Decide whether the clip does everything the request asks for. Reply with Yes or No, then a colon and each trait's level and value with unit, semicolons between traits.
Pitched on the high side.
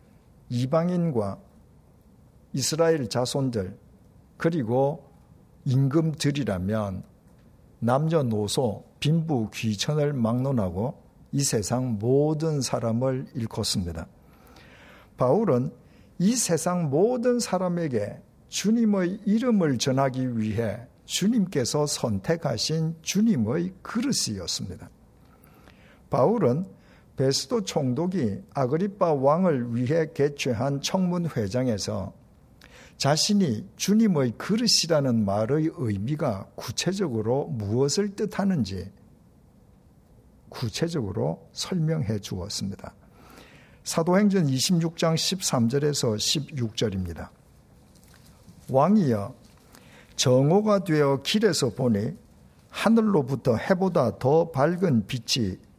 No: medium, 140 Hz